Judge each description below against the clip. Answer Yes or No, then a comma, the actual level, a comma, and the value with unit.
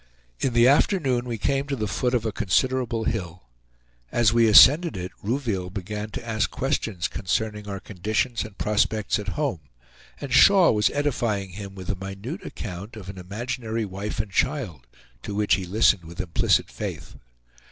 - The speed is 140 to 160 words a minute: No, average, 170 wpm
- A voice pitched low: Yes, low, 110 Hz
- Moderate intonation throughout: Yes, average, 4.2 semitones